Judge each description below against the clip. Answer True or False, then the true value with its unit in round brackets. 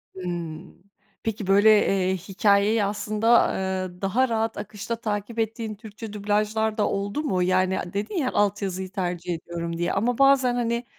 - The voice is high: True (205 Hz)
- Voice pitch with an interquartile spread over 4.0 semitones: False (3.0 semitones)